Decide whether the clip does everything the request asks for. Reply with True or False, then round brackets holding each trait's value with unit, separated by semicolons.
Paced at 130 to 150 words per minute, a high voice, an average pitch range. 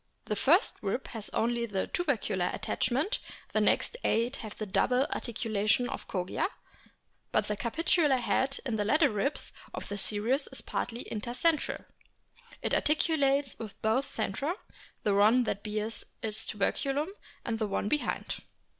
True (145 wpm; 235 Hz; 4.7 semitones)